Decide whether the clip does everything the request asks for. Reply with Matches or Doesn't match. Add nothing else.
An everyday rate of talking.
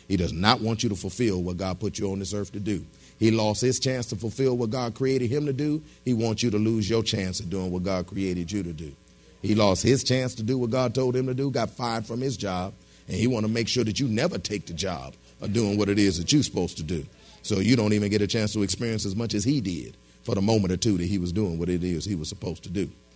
Doesn't match